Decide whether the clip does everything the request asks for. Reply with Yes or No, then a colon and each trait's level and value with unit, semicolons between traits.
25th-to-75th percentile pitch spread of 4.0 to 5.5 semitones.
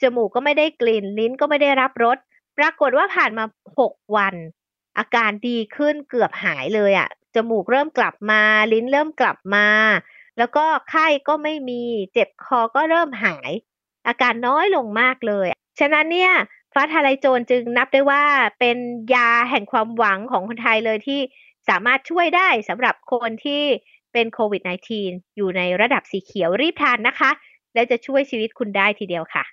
Yes: average, 4.3 semitones